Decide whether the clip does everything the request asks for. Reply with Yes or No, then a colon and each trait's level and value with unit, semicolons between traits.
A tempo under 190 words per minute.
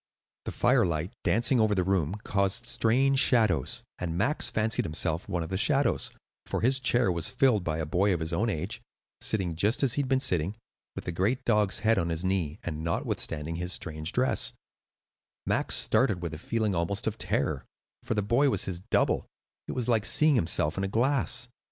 No: average, 195 wpm